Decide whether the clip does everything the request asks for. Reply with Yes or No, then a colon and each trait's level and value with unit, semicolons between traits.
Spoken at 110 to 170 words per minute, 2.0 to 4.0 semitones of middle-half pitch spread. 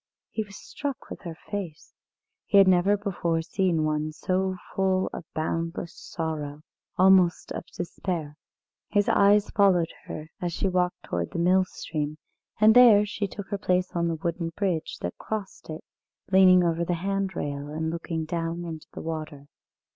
Yes: average, 160 wpm; average, 3.2 semitones